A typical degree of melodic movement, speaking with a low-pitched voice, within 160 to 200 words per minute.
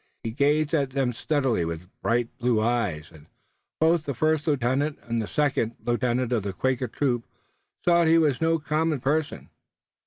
Yes: average, 4.6 semitones; low, 130 Hz; average, 175 wpm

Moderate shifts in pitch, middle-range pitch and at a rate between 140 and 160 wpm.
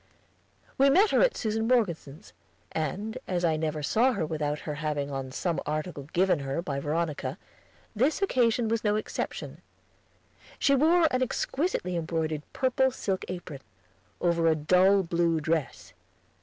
No: wide, 6.9 semitones; medium, 175 Hz; average, 145 wpm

